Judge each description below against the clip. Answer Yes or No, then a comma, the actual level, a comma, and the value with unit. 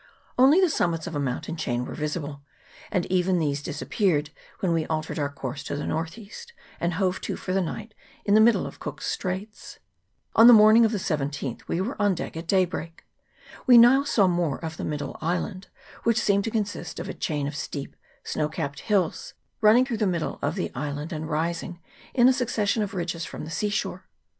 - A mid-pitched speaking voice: Yes, medium, 175 Hz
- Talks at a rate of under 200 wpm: No, fast, 205 wpm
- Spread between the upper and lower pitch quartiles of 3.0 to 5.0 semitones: No, wide, 5.4 semitones